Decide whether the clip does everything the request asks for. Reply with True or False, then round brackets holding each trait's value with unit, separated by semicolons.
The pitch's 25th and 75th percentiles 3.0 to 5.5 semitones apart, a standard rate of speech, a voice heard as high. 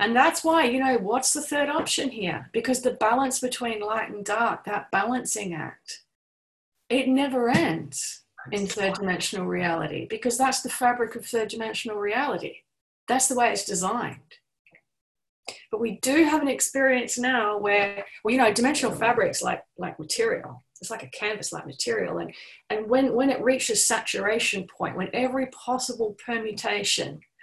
True (3.8 semitones; 160 wpm; 240 Hz)